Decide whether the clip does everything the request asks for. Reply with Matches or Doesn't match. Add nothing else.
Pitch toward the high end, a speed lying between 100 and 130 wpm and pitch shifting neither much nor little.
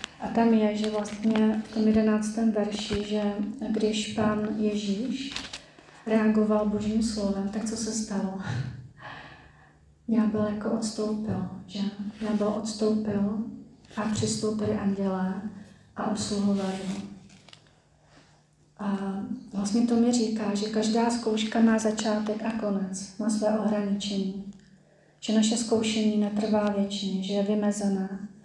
Doesn't match